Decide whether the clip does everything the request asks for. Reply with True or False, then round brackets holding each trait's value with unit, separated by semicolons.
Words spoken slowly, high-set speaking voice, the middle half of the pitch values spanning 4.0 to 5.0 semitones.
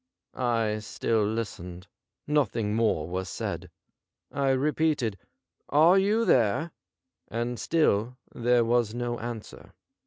False (120 wpm; 120 Hz; 4.5 semitones)